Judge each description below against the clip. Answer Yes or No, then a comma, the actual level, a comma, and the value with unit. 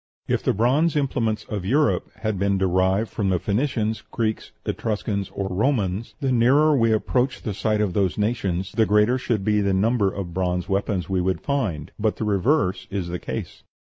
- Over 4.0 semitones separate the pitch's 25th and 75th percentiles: No, average, 3.7 semitones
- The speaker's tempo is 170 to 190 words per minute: Yes, average, 185 wpm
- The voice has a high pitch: No, low, 105 Hz